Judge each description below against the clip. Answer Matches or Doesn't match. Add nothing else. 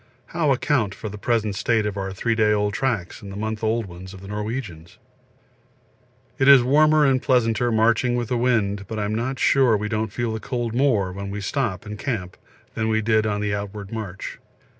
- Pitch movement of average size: Matches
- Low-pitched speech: Matches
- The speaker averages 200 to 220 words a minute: Matches